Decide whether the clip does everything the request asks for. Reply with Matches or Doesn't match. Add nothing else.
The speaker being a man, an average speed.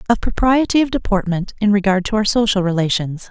Doesn't match